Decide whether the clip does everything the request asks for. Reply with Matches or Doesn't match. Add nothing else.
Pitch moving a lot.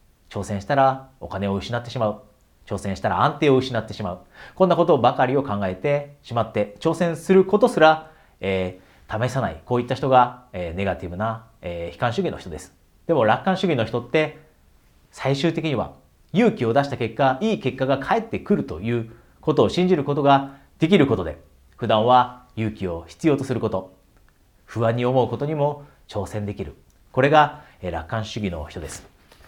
Matches